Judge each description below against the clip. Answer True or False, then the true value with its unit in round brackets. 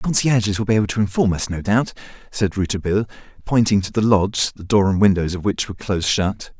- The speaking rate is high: True (230 wpm)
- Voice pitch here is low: True (100 Hz)